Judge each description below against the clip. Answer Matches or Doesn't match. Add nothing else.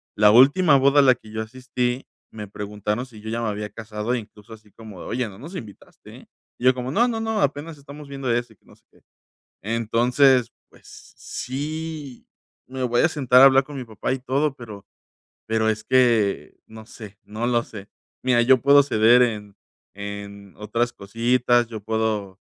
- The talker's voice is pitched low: Matches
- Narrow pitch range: Doesn't match